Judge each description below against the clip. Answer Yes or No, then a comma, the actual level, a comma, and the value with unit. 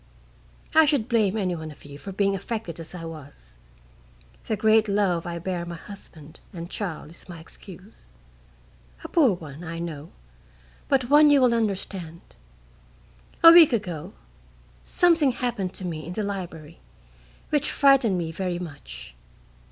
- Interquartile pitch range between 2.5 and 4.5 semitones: No, average, 5.2 semitones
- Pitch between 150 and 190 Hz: Yes, medium, 185 Hz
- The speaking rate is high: No, average, 150 wpm